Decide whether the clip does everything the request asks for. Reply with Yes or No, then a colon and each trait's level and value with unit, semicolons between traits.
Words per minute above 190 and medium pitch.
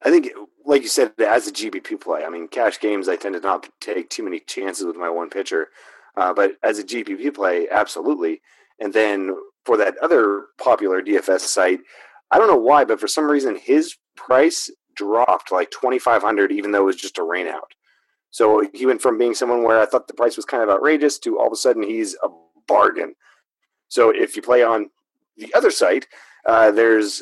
No: fast, 205 wpm; very high, 330 Hz